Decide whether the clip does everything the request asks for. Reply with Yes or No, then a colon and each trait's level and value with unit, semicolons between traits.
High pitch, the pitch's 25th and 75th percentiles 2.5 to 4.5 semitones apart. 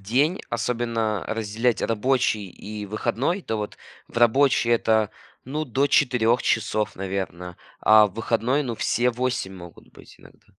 No: low, 115 Hz; average, 2.9 semitones